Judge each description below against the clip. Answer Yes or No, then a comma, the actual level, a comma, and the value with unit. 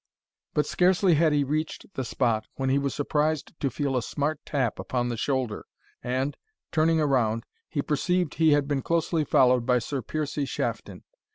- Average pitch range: Yes, average, 3.2 semitones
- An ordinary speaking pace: Yes, average, 175 wpm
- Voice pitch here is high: No, medium, 140 Hz